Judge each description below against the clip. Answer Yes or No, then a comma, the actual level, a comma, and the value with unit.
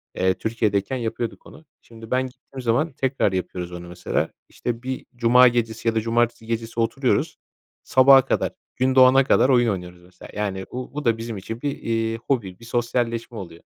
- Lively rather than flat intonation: No, average, 3.2 semitones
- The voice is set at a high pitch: No, low, 115 Hz